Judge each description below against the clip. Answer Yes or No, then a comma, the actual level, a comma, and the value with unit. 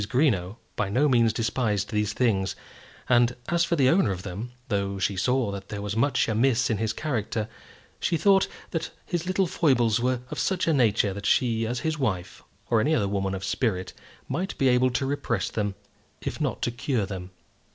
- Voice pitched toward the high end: No, low, 115 Hz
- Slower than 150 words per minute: No, average, 195 wpm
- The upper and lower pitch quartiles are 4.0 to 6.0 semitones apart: Yes, average, 4.9 semitones